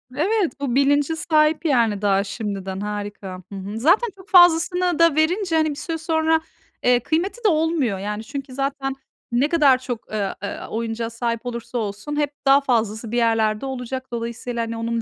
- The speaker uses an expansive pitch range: Yes, wide, 5.9 semitones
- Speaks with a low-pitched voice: No, very high, 255 Hz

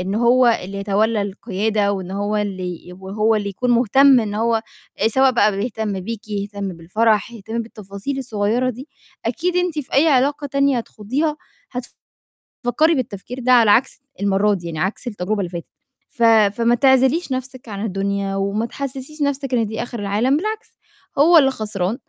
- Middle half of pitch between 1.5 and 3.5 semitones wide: No, average, 4.4 semitones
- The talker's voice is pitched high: Yes, high, 225 Hz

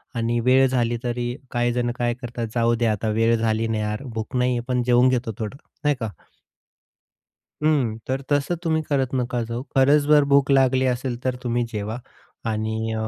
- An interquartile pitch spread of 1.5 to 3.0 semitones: Yes, narrow, 2.4 semitones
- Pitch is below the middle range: Yes, low, 120 Hz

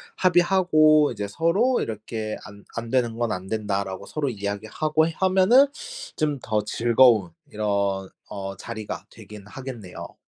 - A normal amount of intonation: No, wide, 7.1 semitones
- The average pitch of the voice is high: No, low, 115 Hz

